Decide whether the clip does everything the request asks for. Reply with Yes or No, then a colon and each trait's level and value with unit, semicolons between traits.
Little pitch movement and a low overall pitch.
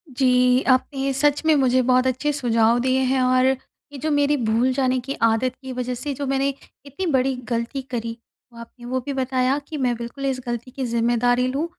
No: narrow, 1.8 semitones; very high, 255 Hz